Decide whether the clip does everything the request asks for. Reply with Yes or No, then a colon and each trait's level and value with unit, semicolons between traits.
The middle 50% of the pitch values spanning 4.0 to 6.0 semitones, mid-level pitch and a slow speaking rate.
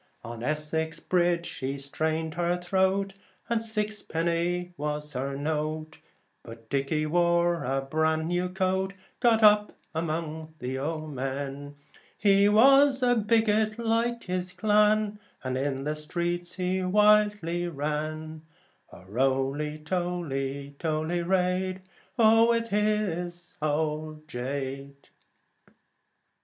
Yes: average, 4.6 semitones; medium, 170 Hz; slow, 110 wpm